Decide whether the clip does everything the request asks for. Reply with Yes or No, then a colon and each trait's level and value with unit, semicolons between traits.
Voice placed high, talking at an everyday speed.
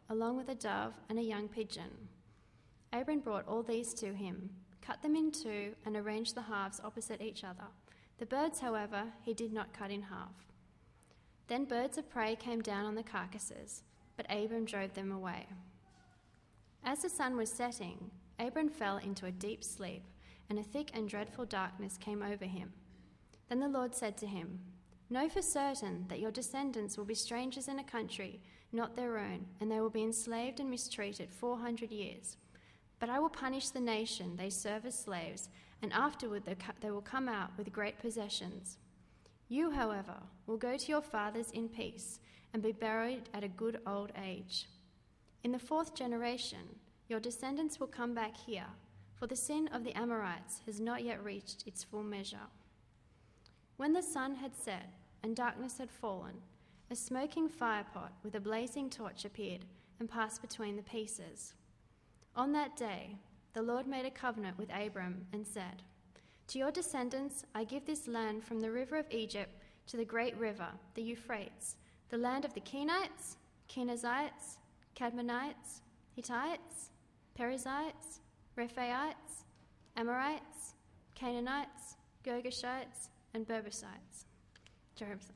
Yes: high, 225 Hz; average, 160 wpm